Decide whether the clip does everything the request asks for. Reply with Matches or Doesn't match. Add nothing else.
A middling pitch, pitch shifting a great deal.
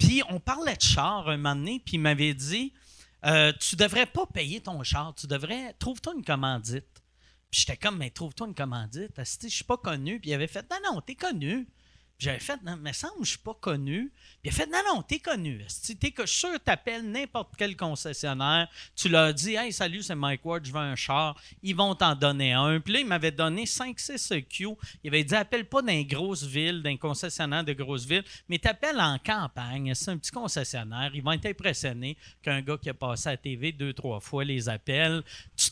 Matches